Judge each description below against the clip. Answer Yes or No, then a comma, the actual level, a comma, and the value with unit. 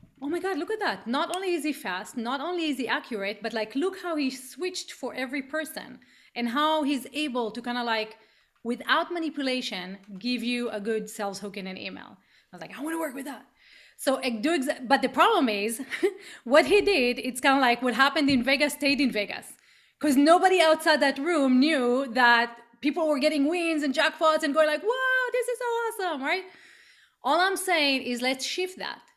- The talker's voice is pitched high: Yes, very high, 280 Hz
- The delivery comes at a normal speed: No, fast, 210 wpm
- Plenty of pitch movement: No, average, 5.0 semitones